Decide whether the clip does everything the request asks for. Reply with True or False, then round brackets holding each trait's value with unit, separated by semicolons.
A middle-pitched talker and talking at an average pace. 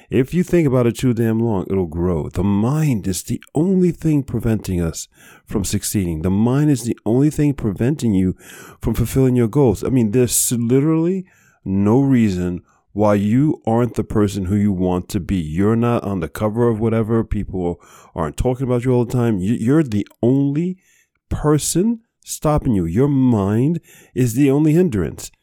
False (115 Hz; 175 wpm)